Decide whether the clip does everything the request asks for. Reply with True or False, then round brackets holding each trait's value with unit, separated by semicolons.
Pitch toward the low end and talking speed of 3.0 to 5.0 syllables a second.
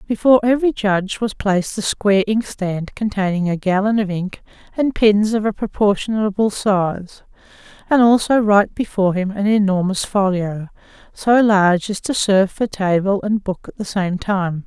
False (200 Hz; 4.9 syllables/s)